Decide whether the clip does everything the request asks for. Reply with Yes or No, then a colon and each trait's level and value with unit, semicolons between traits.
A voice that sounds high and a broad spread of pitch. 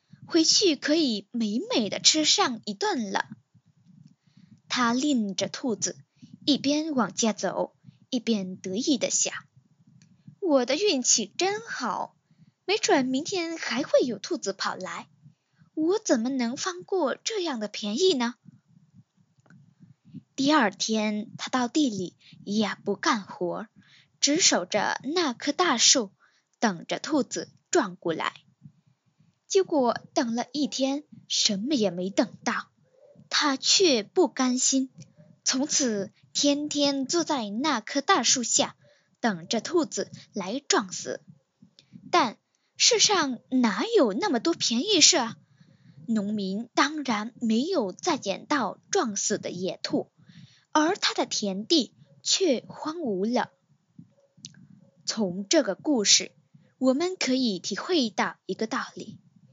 Yes: high, 240 Hz; wide, 7.6 semitones